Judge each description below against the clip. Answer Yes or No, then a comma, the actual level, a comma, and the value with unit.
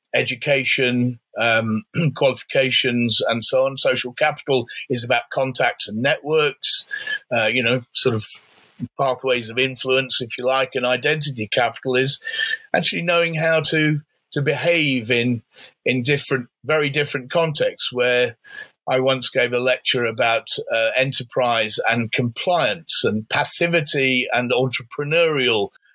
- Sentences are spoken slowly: Yes, slow, 125 wpm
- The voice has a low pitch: Yes, low, 130 Hz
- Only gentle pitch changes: No, average, 3.9 semitones